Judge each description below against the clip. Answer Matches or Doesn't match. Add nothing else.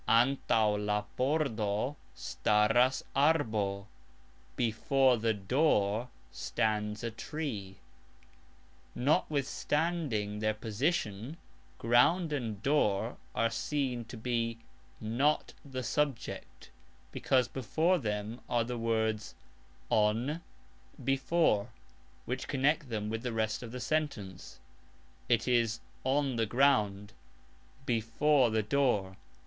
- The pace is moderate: Doesn't match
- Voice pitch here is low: Matches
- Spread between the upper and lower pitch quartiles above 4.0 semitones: Matches